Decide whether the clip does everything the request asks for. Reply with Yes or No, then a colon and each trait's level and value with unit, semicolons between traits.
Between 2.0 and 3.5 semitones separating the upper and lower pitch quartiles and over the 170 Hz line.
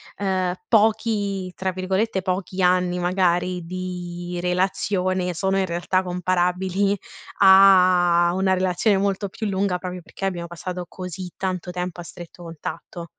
No: narrow, 1.3 semitones; medium, 185 Hz